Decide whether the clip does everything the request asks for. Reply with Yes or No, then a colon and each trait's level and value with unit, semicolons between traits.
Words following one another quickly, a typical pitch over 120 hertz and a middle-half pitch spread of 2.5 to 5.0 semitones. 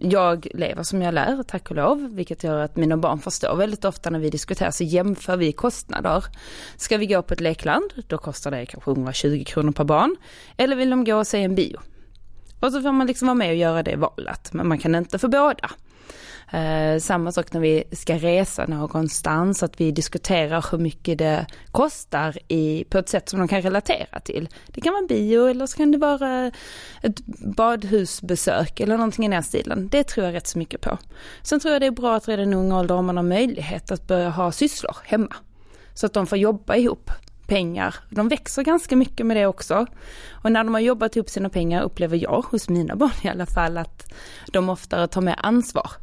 No: fast, 220 wpm; medium, 185 Hz; wide, 5.4 semitones